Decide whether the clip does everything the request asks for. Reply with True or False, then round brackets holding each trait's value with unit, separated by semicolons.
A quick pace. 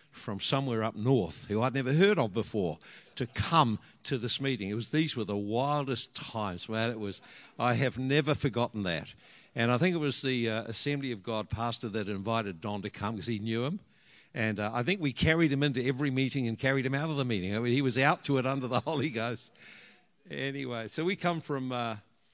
True (225 wpm)